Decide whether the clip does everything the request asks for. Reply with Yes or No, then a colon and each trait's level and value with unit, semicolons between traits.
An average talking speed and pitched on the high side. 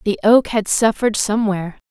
Yes: average, 155 wpm; high, 220 Hz